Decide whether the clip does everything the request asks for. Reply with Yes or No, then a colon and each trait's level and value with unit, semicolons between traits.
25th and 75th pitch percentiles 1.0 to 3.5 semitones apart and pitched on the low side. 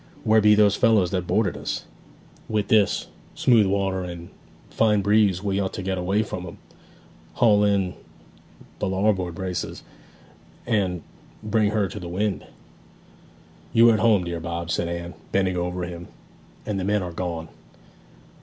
Yes: average, 2.9 semitones; very low, 95 Hz